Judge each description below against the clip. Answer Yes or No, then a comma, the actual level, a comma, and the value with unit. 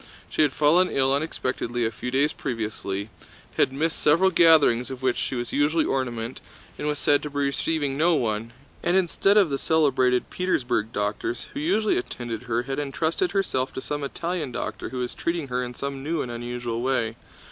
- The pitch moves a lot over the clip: No, average, 4.5 semitones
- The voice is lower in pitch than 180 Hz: Yes, low, 135 Hz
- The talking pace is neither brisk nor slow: Yes, average, 190 wpm